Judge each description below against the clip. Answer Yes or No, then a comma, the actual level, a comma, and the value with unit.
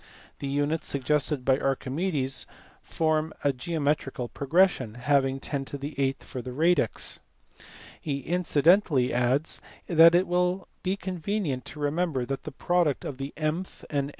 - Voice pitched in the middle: Yes, medium, 145 Hz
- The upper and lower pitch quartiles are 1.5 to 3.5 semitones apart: No, average, 4.0 semitones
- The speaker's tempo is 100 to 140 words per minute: Yes, slow, 135 wpm